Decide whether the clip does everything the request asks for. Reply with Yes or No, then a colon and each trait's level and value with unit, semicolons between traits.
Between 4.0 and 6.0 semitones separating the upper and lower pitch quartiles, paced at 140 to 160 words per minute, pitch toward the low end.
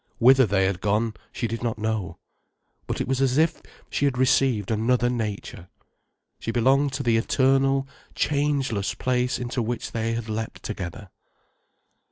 No: average, 3.4 semitones; average, 155 wpm; low, 120 Hz